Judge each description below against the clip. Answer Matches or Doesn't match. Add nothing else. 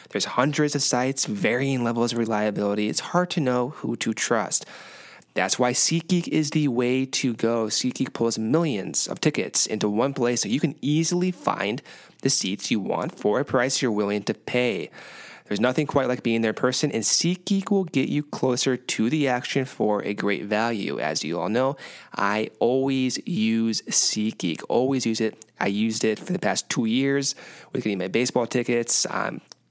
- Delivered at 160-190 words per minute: Matches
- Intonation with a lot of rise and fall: Doesn't match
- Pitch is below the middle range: Matches